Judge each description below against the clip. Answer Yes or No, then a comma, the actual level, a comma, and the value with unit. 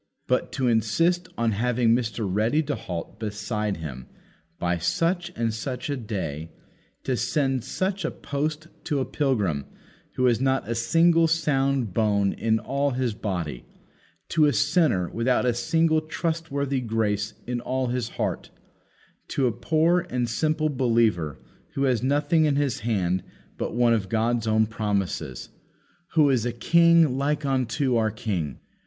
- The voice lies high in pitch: No, low, 125 Hz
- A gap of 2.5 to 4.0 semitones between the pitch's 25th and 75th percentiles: No, average, 5.0 semitones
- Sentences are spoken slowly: No, average, 155 wpm